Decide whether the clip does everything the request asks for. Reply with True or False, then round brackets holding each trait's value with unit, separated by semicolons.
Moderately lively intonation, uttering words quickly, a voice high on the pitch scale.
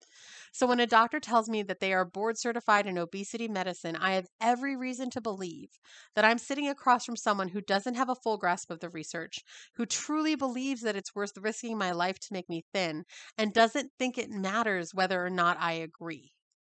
True (4.5 semitones; 210 wpm; 210 Hz)